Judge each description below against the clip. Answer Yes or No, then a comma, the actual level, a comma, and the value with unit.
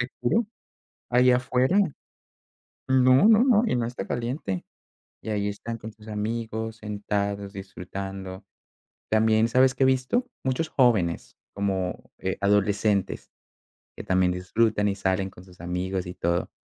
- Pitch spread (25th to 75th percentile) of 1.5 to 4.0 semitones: No, average, 4.4 semitones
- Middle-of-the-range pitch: No, low, 105 Hz